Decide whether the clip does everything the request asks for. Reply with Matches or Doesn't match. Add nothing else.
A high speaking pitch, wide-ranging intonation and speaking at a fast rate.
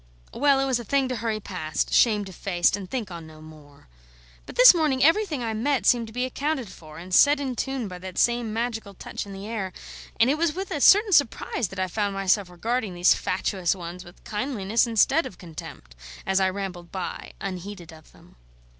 Matches